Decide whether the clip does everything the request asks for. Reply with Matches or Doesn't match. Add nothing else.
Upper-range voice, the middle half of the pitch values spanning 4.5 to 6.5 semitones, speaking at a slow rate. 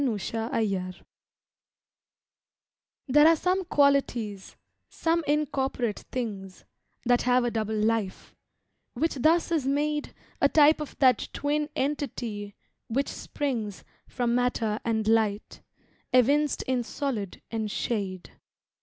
Matches